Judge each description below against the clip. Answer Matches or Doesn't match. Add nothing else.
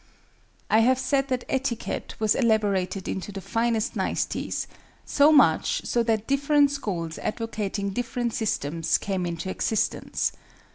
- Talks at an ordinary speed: Doesn't match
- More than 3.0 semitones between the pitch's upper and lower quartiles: Matches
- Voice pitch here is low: Doesn't match